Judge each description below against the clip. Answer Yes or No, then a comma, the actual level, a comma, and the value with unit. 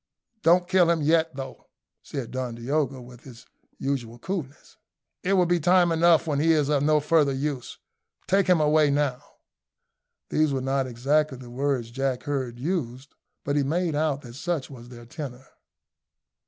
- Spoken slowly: No, average, 170 wpm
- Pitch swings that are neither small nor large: Yes, average, 3.8 semitones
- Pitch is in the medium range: Yes, medium, 145 Hz